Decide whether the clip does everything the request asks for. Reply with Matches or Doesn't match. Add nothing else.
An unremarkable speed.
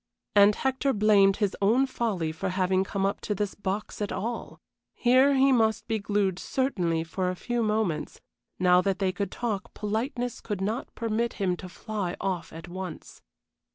Matches